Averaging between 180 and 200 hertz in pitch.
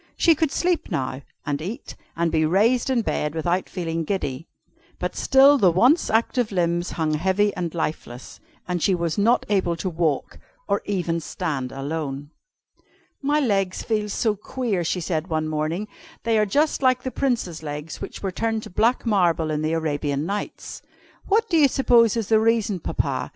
Yes: medium, 185 Hz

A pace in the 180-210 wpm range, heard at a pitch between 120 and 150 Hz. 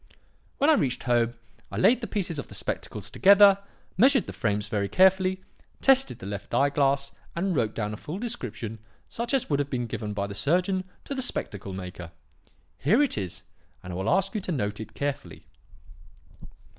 Yes: average, 190 wpm; medium, 140 Hz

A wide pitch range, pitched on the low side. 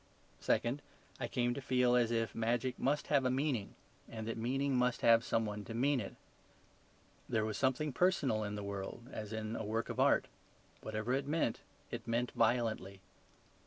No: average, 3.0 semitones; low, 120 Hz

